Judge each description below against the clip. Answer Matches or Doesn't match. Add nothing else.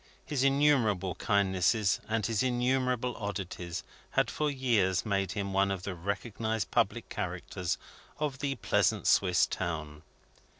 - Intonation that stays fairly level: Doesn't match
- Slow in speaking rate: Matches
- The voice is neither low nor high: Doesn't match